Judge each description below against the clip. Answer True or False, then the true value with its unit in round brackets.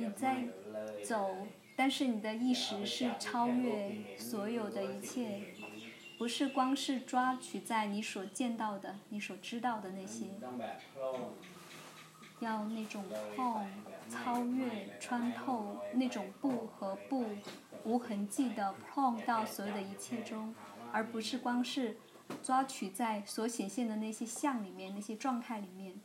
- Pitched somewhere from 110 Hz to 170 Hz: False (220 Hz)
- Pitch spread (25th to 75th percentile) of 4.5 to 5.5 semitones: False (3.6 semitones)